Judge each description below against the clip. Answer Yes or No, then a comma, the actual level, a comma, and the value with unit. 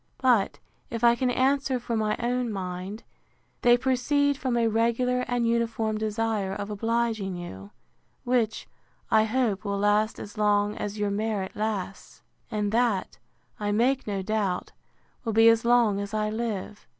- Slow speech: No, average, 155 wpm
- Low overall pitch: No, high, 220 Hz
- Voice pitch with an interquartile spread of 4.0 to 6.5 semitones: No, narrow, 2.6 semitones